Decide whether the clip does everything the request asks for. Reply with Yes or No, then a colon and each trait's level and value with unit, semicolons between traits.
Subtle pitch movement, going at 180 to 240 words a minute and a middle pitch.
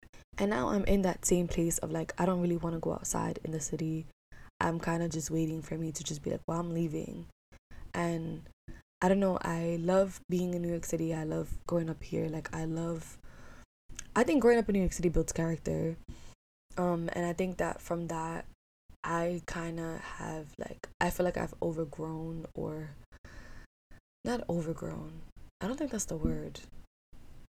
Yes: narrow, 1.8 semitones; average, 190 wpm; medium, 165 Hz